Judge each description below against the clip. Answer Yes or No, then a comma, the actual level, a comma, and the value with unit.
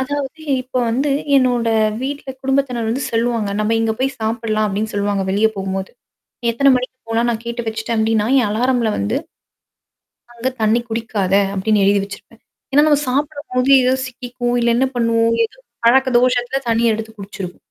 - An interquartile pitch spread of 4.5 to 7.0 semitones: No, average, 2.8 semitones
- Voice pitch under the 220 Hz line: No, high, 235 Hz